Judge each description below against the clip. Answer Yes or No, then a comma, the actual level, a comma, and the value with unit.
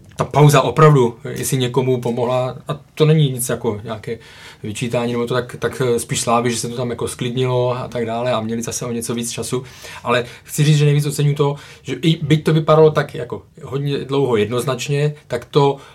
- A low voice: Yes, low, 130 Hz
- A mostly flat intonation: No, average, 3.5 semitones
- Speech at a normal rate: No, fast, 205 wpm